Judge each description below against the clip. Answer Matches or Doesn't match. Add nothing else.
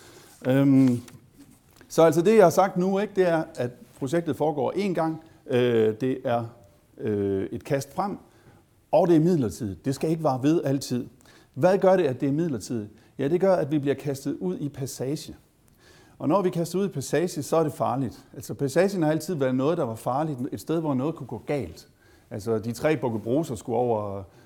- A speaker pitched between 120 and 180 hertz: Matches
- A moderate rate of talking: Matches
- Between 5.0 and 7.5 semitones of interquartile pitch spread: Matches